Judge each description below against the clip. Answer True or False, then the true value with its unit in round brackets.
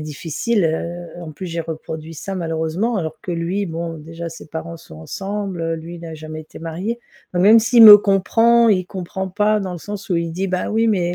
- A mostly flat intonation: False (3.6 semitones)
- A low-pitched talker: False (175 Hz)